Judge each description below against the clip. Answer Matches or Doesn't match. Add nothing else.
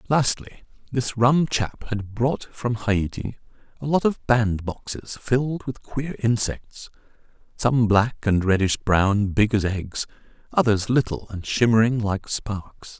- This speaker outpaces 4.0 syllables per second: Doesn't match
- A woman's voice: Doesn't match